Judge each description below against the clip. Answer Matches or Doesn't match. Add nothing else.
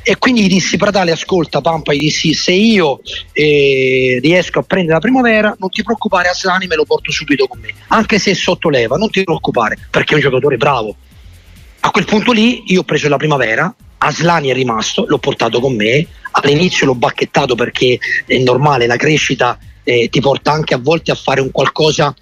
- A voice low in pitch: Doesn't match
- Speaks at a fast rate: Matches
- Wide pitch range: Matches